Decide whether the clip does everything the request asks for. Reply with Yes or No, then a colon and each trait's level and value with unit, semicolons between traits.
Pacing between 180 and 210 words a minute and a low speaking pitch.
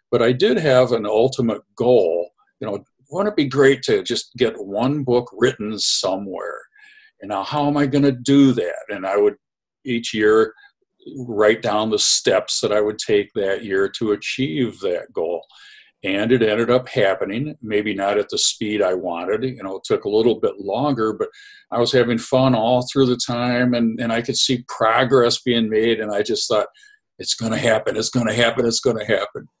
Yes: fast, 205 wpm; low, 125 Hz